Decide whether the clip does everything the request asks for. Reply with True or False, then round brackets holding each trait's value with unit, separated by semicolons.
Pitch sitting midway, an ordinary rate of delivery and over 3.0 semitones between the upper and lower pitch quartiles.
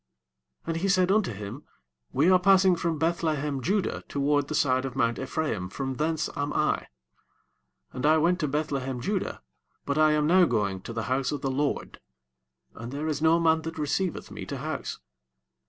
True (150 Hz; 185 wpm; 3.8 semitones)